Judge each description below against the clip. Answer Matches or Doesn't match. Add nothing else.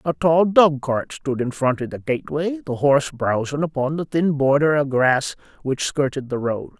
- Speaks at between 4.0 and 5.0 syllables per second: Matches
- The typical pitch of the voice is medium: Matches